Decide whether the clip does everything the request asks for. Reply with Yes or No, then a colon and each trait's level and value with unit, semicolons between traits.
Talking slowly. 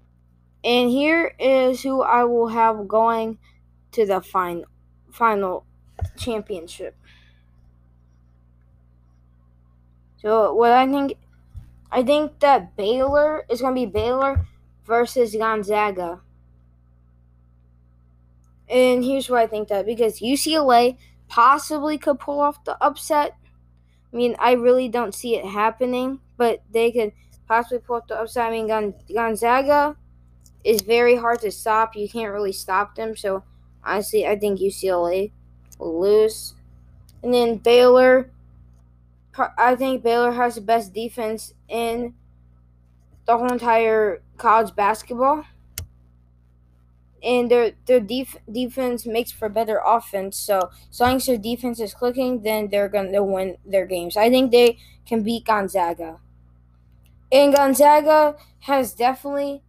Yes: slow, 130 wpm